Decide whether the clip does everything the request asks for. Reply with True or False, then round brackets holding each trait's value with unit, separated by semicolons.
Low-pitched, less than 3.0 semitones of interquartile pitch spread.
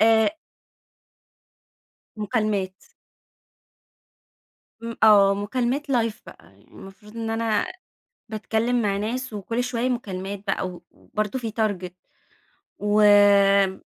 False (215 Hz; 2.5 semitones)